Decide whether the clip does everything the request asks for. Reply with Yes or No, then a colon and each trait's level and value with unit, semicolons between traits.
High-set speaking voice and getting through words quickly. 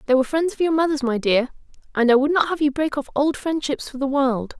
Yes: very high, 285 Hz; fast, 275 wpm